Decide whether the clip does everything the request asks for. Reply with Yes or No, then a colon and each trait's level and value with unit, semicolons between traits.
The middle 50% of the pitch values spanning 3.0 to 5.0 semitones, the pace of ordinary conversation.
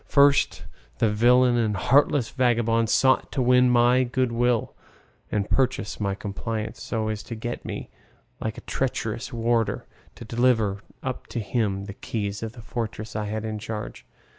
No: narrow, 2.4 semitones; average, 165 wpm